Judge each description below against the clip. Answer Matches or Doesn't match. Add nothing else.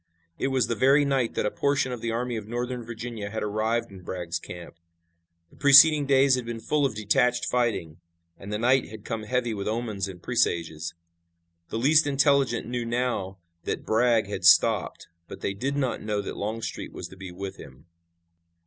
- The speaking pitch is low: Matches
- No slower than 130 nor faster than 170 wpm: Doesn't match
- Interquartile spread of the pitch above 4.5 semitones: Doesn't match